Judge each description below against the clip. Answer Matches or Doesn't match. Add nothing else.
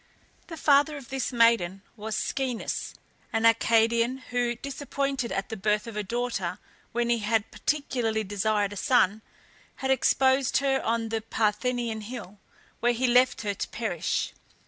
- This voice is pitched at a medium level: Doesn't match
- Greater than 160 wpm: Doesn't match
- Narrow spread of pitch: Doesn't match